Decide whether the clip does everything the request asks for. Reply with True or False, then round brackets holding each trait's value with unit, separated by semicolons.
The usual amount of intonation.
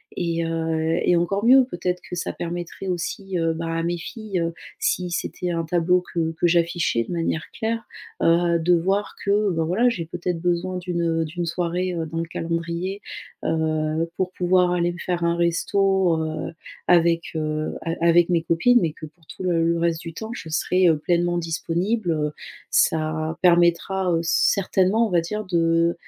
False (1.7 semitones)